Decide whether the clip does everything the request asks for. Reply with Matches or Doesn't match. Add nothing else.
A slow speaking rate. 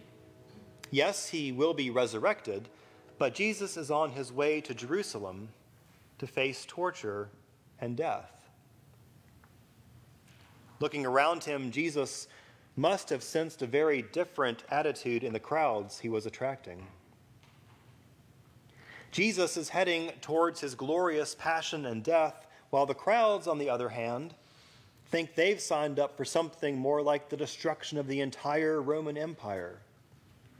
Matches